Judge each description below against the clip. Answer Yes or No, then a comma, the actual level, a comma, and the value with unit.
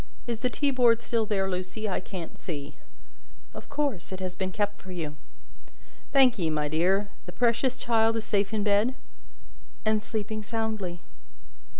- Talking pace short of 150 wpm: No, average, 160 wpm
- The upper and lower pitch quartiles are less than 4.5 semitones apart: Yes, average, 3.8 semitones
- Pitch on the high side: Yes, high, 210 Hz